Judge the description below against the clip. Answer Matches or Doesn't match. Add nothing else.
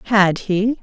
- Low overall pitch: Doesn't match